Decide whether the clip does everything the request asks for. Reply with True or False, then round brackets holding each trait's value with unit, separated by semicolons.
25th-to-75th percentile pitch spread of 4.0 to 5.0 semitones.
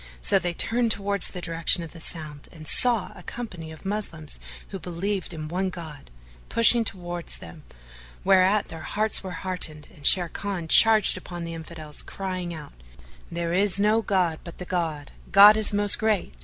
False (3.6 semitones)